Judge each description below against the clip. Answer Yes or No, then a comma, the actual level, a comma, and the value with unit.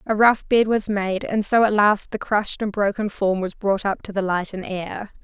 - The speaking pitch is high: Yes, high, 205 Hz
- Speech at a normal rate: No, fast, 250 wpm